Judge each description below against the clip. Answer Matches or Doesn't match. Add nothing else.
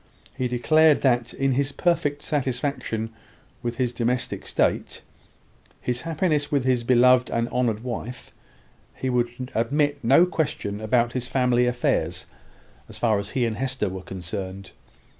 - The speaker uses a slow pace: Doesn't match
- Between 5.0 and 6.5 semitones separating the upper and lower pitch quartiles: Doesn't match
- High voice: Doesn't match